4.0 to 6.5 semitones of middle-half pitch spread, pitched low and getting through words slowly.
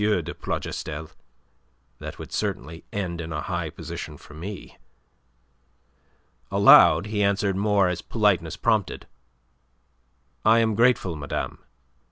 Yes: average, 4.3 semitones; very low, 95 Hz; slow, 115 wpm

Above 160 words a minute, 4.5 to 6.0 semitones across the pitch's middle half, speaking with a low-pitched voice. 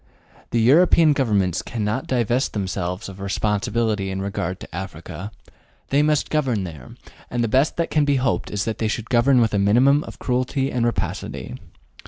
Yes: average, 175 wpm; average, 5.2 semitones; low, 115 Hz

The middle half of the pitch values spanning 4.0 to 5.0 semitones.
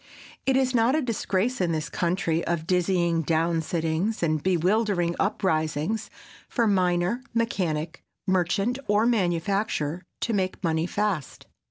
Yes: average, 4.3 semitones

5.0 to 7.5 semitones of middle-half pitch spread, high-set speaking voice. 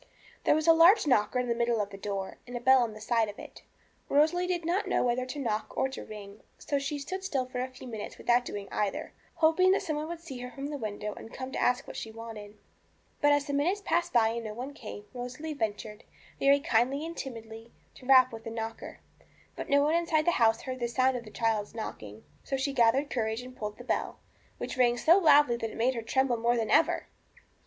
No: average, 4.3 semitones; very high, 250 Hz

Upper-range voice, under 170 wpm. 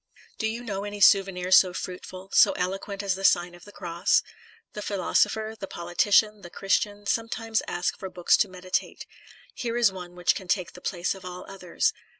No: high, 195 Hz; average, 185 wpm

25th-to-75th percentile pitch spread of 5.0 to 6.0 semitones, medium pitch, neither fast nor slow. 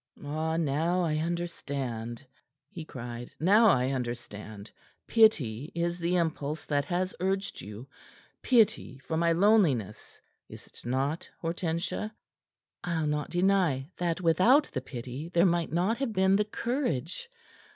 No: wide, 5.5 semitones; medium, 165 Hz; slow, 130 wpm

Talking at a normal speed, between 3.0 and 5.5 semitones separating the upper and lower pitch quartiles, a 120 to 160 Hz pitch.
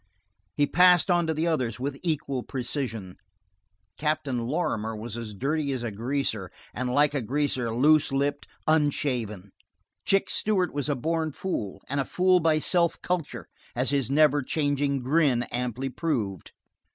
Yes: average, 150 wpm; average, 4.4 semitones; medium, 140 Hz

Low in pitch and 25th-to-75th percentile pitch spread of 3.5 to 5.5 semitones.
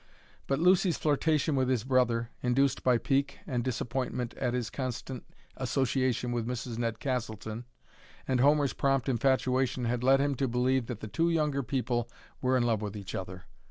No: low, 125 Hz; narrow, 2.4 semitones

